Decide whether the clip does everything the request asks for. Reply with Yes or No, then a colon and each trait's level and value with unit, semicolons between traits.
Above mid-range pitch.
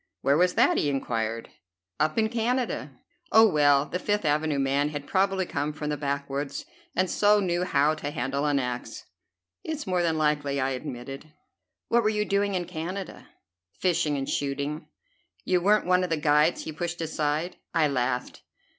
No: medium, 155 Hz